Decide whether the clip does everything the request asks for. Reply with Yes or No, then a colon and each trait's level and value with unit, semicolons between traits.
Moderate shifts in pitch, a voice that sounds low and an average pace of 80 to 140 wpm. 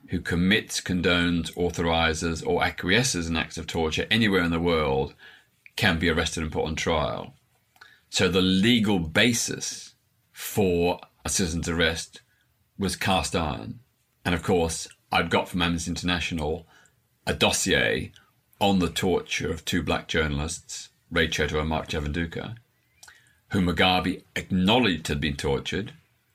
Yes: average, 3.2 semitones; very low, 90 Hz; slow, 135 wpm